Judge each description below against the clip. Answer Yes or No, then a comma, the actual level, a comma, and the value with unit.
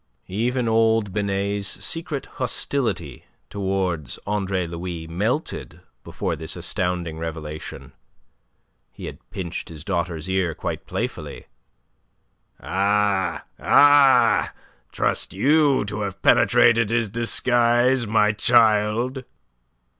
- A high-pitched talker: No, low, 105 Hz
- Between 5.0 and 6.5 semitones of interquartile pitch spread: No, average, 4.5 semitones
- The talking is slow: Yes, slow, 95 wpm